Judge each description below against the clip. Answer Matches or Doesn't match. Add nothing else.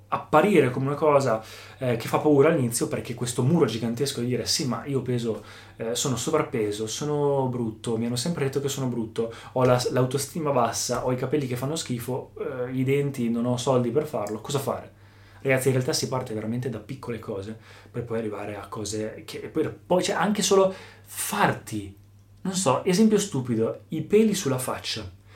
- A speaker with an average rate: Doesn't match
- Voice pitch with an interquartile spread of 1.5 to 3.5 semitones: Doesn't match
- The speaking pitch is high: Doesn't match